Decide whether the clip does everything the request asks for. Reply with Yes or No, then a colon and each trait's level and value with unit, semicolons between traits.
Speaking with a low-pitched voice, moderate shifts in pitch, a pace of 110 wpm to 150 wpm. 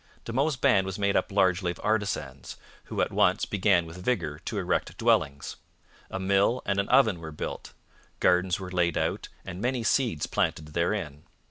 No: very low, 95 Hz; average, 3.6 semitones; average, 175 wpm